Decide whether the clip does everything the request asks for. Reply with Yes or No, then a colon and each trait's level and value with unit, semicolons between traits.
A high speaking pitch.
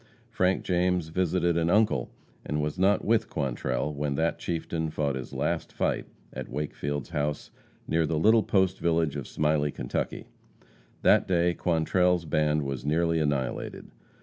No: very low, 80 Hz